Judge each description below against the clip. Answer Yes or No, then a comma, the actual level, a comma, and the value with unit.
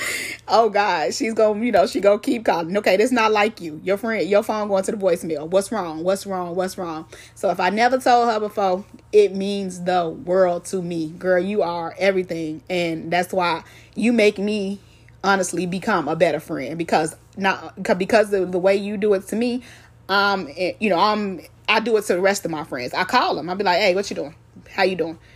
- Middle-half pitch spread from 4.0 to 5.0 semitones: No, average, 2.9 semitones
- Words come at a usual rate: No, fast, 230 wpm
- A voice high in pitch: Yes, high, 195 Hz